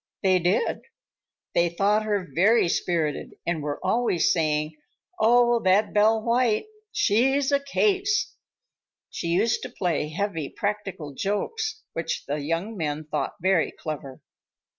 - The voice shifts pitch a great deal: Yes, wide, 6.0 semitones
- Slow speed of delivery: Yes, slow, 130 wpm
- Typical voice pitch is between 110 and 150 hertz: No, high, 195 Hz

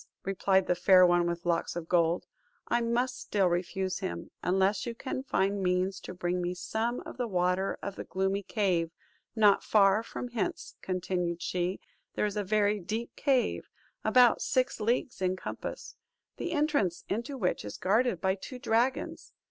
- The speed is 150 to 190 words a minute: Yes, average, 170 wpm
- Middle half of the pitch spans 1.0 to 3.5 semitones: No, average, 4.3 semitones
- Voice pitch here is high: Yes, high, 195 Hz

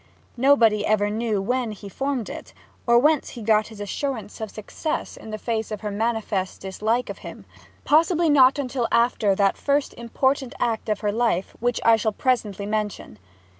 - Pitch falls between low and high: No, high, 225 Hz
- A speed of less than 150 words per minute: No, average, 175 wpm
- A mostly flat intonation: No, average, 3.4 semitones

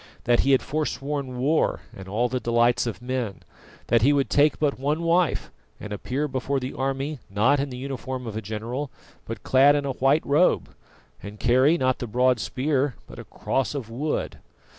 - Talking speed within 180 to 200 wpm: Yes, average, 190 wpm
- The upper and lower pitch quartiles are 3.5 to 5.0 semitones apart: No, average, 2.9 semitones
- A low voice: Yes, low, 130 Hz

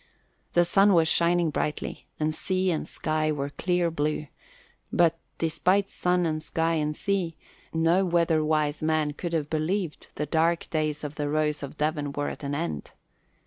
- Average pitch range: No, narrow, 2.2 semitones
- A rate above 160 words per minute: Yes, average, 170 wpm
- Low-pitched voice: No, medium, 155 Hz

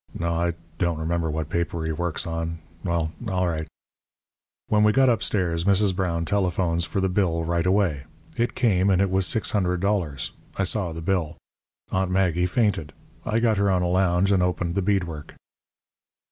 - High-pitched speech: No, very low, 90 Hz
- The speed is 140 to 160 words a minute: No, average, 175 wpm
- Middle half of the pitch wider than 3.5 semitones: No, average, 2.8 semitones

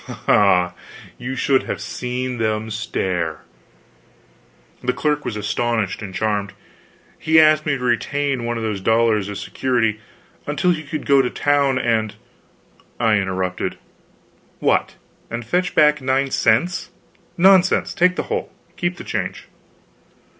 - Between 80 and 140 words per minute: Yes, slow, 135 wpm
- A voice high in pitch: No, low, 120 Hz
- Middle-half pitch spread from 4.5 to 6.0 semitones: Yes, average, 5.1 semitones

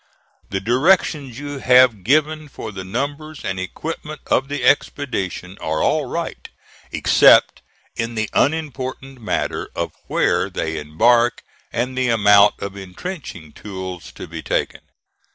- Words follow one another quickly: No, slow, 135 wpm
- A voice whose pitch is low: Yes, low, 120 Hz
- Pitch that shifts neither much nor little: No, wide, 6.6 semitones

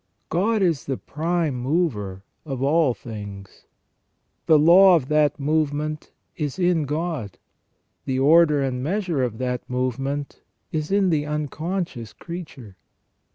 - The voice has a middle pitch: Yes, medium, 150 Hz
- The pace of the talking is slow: Yes, slow, 125 wpm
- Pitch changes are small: No, average, 4.6 semitones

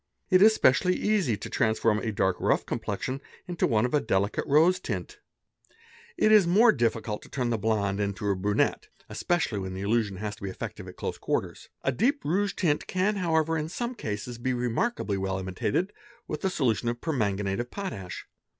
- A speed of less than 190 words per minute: No, average, 195 wpm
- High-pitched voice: No, low, 120 Hz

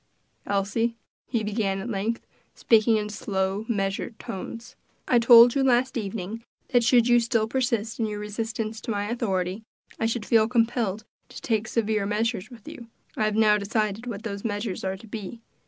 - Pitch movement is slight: Yes, narrow, 2.3 semitones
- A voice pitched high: Yes, high, 220 Hz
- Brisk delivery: No, average, 175 wpm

